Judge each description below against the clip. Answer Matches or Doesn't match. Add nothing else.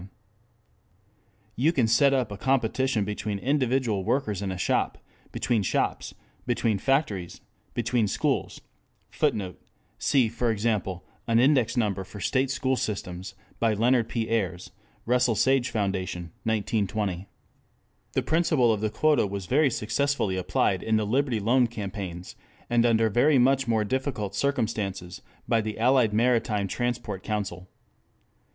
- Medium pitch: Doesn't match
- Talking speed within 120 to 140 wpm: Matches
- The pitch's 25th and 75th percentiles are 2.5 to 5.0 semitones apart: Matches